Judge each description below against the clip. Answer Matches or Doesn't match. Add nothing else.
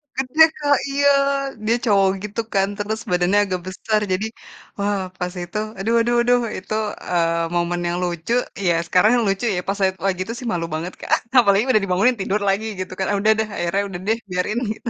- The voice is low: Doesn't match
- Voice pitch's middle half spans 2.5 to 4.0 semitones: Matches